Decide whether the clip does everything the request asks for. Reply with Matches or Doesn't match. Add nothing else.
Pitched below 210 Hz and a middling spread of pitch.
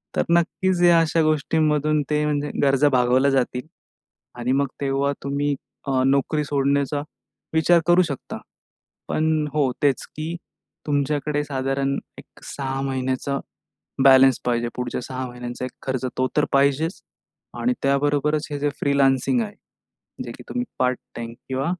Doesn't match